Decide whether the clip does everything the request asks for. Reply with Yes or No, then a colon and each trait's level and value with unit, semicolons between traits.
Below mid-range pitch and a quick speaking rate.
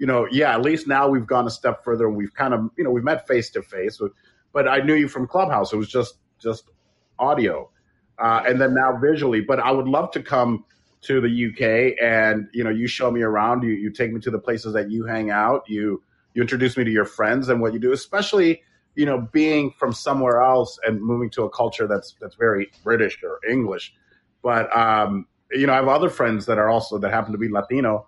Yes: low, 120 Hz; fast, 235 wpm